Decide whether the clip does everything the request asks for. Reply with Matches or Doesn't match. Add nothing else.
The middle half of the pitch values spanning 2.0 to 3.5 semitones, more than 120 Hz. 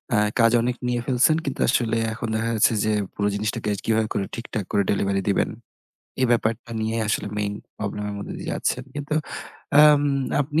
Doesn't match